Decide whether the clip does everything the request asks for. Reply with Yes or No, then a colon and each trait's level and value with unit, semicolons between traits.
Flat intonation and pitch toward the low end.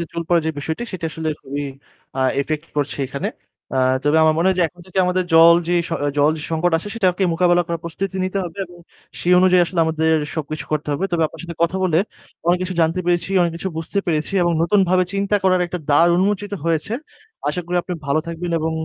No: narrow, 2.3 semitones; medium, 170 Hz